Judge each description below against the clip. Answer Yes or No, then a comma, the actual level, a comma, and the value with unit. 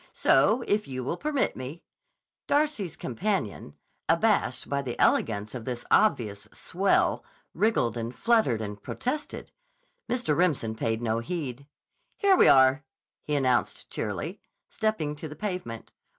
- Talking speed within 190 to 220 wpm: No, slow, 135 wpm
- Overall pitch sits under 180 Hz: Yes, medium, 140 Hz